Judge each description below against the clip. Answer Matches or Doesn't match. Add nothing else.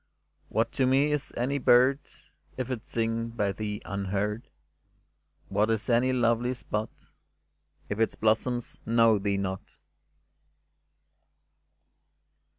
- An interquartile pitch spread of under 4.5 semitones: Matches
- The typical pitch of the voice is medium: Doesn't match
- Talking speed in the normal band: Doesn't match